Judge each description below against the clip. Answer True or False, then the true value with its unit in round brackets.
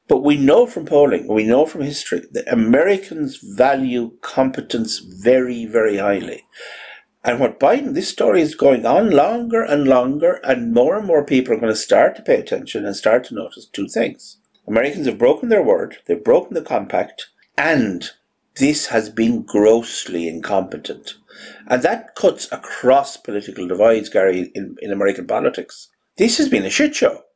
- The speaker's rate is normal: True (170 wpm)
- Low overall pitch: True (130 Hz)